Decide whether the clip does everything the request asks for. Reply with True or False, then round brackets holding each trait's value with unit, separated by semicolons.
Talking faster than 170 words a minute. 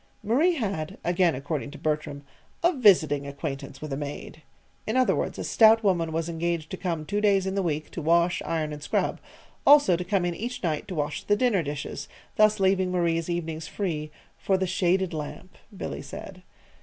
True (195 wpm)